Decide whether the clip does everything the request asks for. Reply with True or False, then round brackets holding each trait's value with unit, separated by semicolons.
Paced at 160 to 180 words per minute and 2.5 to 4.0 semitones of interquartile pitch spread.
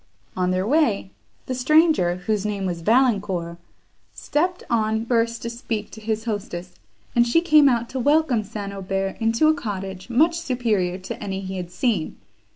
False (165 wpm; 4.8 semitones)